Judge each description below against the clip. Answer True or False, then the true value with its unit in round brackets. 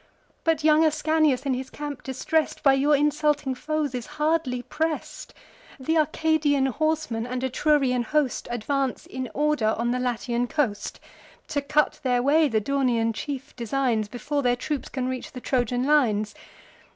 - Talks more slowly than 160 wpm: True (150 wpm)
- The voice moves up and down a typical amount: True (3.4 semitones)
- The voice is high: True (270 Hz)